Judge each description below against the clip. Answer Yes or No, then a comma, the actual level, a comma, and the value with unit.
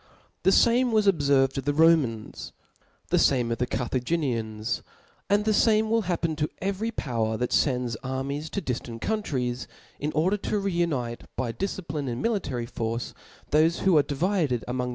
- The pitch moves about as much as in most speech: No, wide, 7.5 semitones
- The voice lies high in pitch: No, medium, 145 Hz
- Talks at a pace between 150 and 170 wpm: Yes, average, 155 wpm